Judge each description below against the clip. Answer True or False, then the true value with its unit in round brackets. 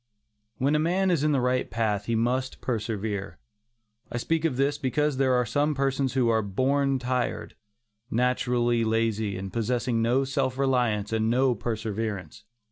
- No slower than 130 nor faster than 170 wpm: True (160 wpm)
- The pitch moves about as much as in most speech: True (3.3 semitones)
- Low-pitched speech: True (125 Hz)